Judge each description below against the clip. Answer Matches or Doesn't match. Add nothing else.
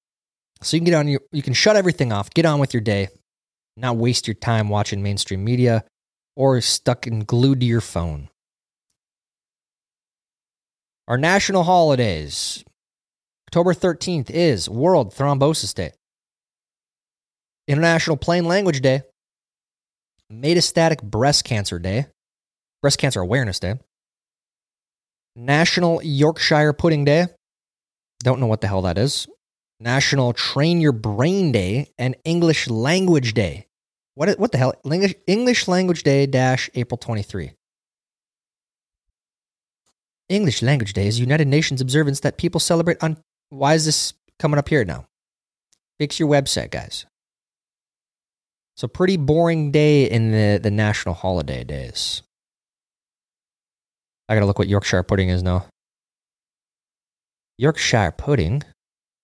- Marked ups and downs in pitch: Matches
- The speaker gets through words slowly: Matches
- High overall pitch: Doesn't match